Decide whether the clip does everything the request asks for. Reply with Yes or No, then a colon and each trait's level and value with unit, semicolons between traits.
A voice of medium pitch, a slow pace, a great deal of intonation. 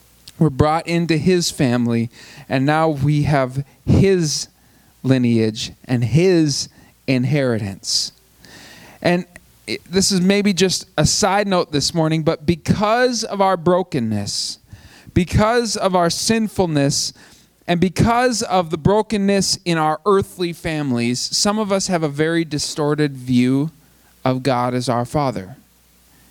Yes: medium, 155 Hz; slow, 125 wpm; wide, 6.2 semitones